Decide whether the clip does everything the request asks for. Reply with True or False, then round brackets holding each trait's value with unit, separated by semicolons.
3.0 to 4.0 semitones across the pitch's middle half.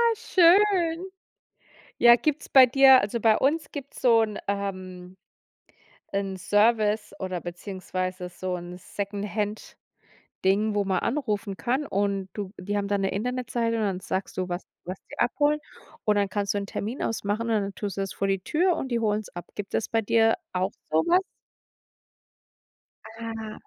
True (3.5 semitones)